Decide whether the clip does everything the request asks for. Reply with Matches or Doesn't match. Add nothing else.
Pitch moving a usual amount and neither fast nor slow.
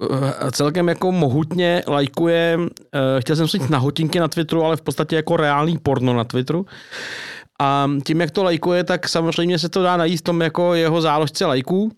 Doesn't match